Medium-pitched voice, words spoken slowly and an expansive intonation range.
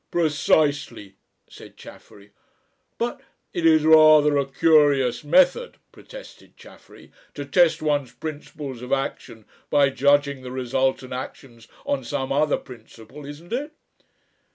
No: medium, 145 Hz; slow, 125 wpm; average, 3.1 semitones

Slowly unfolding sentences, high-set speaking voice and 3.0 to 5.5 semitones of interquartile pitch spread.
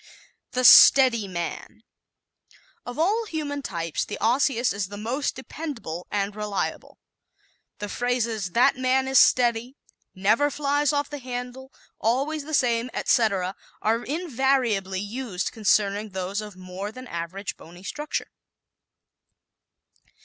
Yes: slow, 125 wpm; high, 235 Hz; average, 5.1 semitones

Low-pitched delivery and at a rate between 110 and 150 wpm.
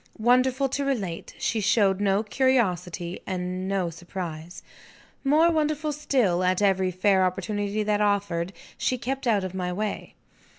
No: high, 200 Hz; average, 140 wpm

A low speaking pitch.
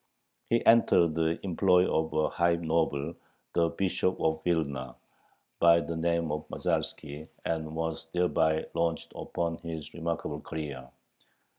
Yes: very low, 80 Hz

